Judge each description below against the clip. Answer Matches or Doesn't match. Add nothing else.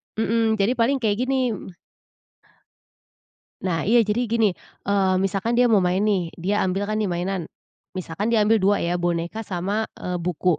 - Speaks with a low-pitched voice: Doesn't match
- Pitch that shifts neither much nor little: Matches